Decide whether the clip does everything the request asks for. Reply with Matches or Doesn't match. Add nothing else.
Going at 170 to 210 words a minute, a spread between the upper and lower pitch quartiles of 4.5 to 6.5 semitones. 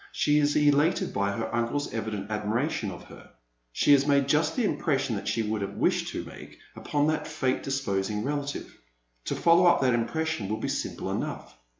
Matches